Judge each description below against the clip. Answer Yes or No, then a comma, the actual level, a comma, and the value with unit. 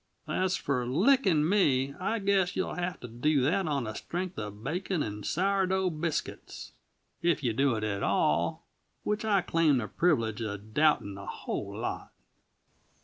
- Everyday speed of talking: Yes, average, 165 wpm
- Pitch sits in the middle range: Yes, medium, 155 Hz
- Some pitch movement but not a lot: No, wide, 8.3 semitones